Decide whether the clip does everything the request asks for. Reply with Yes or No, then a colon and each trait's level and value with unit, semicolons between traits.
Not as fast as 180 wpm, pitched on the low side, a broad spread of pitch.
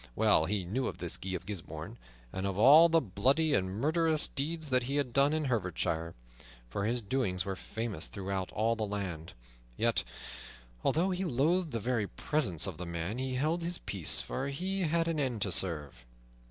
No: average, 190 wpm; low, 120 Hz; wide, 8.1 semitones